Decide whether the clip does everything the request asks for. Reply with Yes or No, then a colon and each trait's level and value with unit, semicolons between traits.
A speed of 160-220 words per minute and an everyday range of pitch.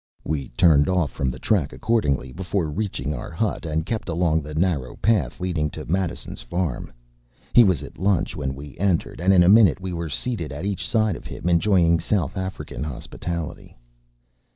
Yes: average, 185 wpm; average, 4.2 semitones